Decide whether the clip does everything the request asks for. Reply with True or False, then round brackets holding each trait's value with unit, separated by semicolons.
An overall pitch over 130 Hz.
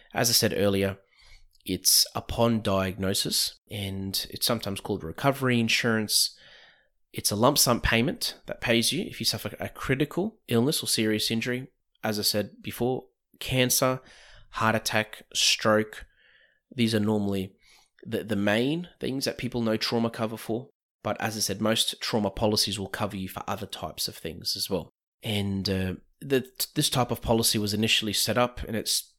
False (110 Hz)